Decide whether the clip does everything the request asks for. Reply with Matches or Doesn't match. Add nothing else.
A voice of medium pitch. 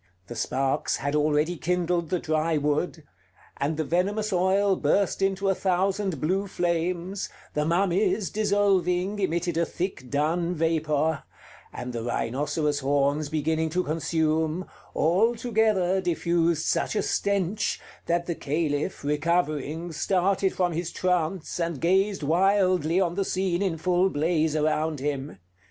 Matches